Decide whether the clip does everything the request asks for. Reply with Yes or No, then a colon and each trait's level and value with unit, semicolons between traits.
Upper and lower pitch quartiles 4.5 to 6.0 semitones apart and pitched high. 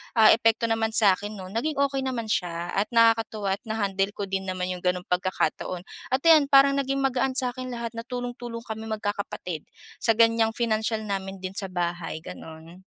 No: average, 4.0 semitones; high, 220 Hz